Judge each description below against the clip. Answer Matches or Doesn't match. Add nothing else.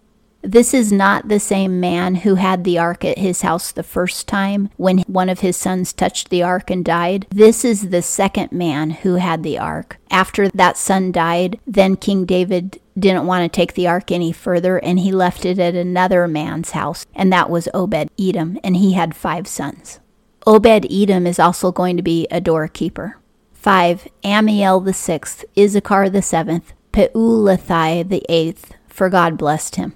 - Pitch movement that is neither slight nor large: Doesn't match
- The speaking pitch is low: Doesn't match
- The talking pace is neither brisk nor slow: Matches